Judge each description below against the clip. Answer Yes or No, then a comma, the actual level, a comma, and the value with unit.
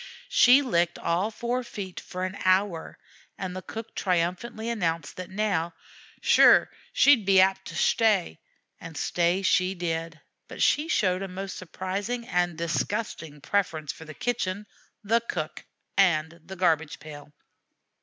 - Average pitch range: Yes, average, 3.6 semitones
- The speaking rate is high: No, average, 145 wpm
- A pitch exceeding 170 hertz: Yes, medium, 185 Hz